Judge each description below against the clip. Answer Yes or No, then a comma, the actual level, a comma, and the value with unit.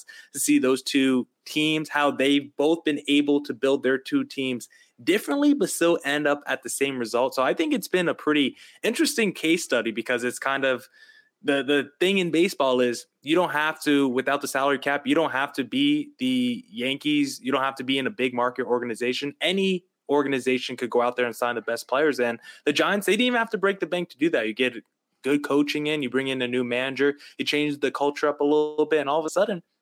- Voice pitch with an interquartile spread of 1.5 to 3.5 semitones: No, average, 4.2 semitones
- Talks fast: Yes, fast, 235 wpm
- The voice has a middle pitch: Yes, medium, 145 Hz